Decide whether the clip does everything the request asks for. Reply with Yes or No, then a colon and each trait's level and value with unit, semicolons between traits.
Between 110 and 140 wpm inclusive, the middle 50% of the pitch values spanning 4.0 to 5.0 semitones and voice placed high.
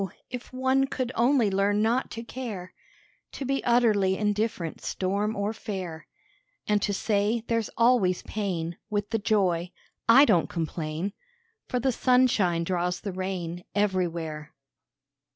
Yes: slow, 135 wpm; average, 4.4 semitones; high, 205 Hz